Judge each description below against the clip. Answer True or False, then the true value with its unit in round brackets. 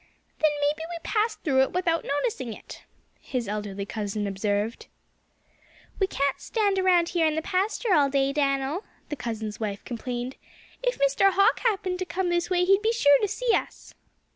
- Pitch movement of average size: False (7.5 semitones)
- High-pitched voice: True (300 Hz)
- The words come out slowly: False (175 wpm)